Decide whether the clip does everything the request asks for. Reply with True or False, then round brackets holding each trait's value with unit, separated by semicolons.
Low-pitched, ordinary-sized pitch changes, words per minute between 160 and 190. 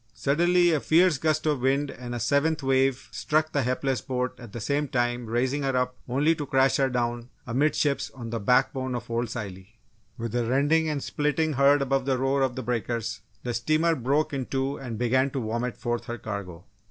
False (130 Hz; 3.0 semitones; 205 wpm)